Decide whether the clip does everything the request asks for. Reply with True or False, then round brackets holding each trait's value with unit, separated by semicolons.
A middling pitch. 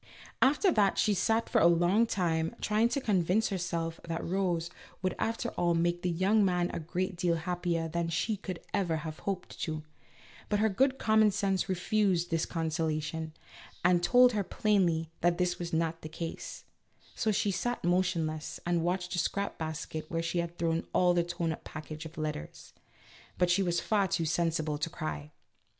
True (175 Hz)